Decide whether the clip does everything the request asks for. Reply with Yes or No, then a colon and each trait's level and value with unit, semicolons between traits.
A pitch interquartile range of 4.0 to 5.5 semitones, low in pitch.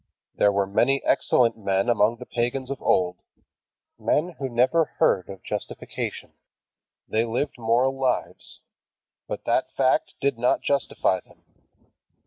Yes: average, 4.6 semitones; low, 120 Hz